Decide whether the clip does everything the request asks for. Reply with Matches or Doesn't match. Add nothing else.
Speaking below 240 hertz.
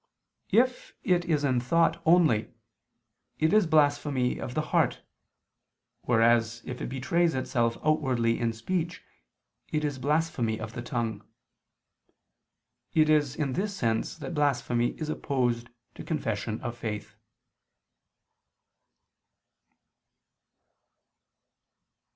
Matches